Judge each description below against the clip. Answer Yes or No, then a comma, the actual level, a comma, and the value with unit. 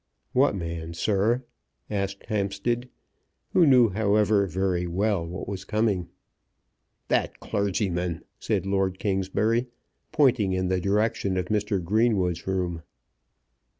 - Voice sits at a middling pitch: No, low, 100 Hz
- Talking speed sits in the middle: No, slow, 115 wpm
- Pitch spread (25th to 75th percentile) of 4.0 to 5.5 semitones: No, average, 2.8 semitones